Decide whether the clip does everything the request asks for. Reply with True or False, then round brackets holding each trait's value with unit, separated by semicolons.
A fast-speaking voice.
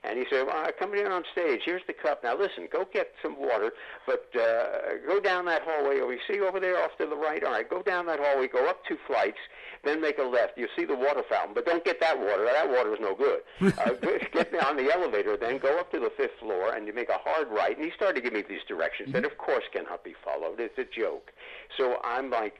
True (265 wpm)